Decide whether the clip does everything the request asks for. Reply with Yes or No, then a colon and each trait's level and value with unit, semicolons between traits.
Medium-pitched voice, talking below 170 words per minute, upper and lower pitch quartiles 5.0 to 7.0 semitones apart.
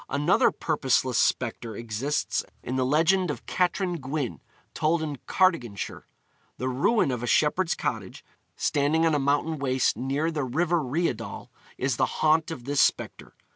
No: medium, 145 Hz; average, 150 wpm; average, 4.0 semitones